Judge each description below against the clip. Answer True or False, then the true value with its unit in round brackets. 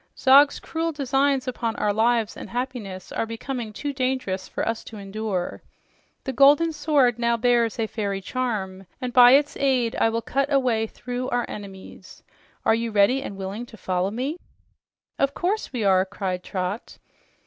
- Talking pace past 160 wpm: True (170 wpm)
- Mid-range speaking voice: False (235 Hz)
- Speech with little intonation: False (4.5 semitones)